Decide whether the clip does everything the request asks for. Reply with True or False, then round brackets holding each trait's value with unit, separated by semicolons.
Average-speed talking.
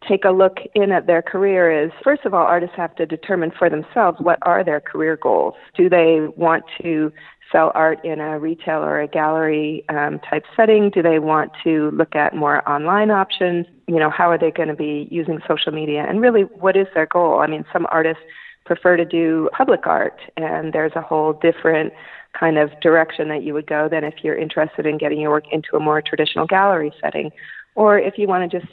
False (215 wpm)